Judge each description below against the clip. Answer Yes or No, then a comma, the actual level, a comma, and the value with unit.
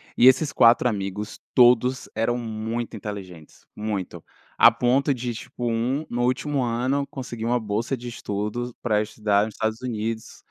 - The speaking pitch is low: Yes, low, 115 Hz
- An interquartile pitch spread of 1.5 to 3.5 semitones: Yes, narrow, 2.5 semitones